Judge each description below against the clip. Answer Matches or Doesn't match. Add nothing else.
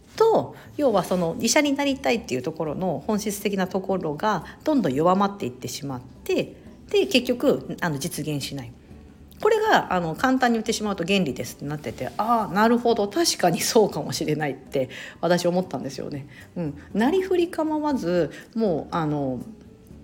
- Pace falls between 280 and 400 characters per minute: Matches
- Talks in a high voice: Matches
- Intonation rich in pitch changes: Matches